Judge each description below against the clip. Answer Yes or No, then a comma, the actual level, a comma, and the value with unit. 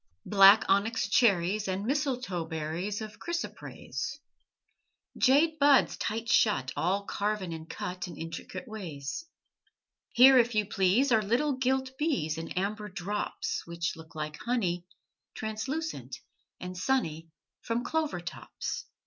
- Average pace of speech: No, slow, 125 wpm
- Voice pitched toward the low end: No, high, 210 Hz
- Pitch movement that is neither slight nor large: No, wide, 6.4 semitones